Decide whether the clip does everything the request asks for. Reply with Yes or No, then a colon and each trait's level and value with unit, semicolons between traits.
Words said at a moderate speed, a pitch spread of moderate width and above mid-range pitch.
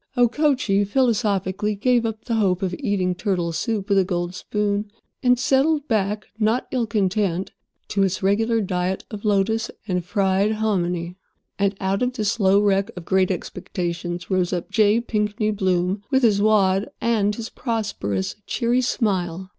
Yes: average, 155 wpm; average, 3.0 semitones; high, 205 Hz